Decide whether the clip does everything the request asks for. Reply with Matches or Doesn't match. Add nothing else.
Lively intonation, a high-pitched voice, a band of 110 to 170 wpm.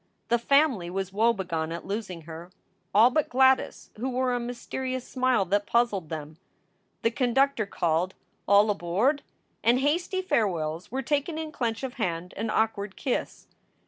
Matches